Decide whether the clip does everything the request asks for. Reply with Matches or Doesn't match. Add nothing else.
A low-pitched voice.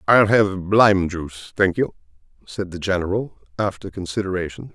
Matches